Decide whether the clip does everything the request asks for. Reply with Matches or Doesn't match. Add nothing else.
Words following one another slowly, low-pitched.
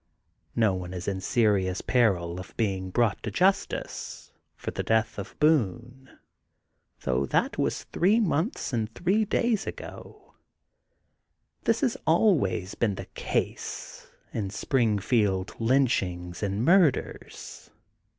Matches